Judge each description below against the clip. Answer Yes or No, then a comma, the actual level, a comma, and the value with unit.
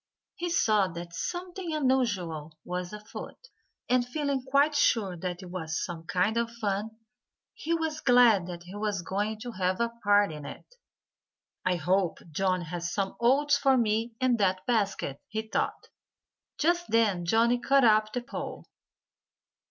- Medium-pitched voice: No, high, 215 Hz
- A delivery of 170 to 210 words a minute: No, average, 155 wpm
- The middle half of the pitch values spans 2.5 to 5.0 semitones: No, wide, 5.4 semitones